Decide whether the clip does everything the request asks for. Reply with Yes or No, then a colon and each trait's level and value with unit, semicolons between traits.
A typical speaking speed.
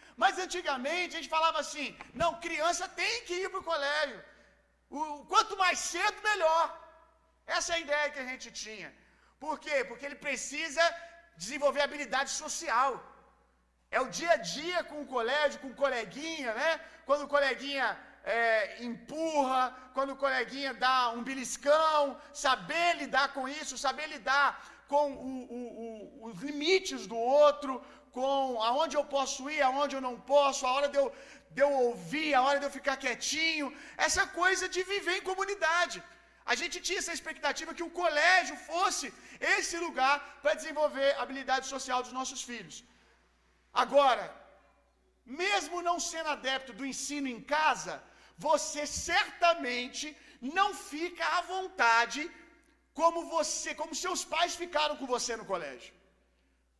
No: fast, 150 wpm